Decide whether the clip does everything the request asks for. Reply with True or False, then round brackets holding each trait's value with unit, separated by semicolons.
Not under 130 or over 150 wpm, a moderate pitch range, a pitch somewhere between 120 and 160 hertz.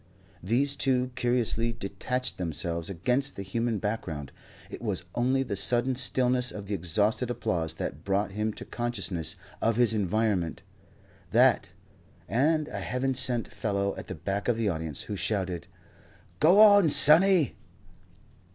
False (140 wpm; 4.6 semitones; 110 Hz)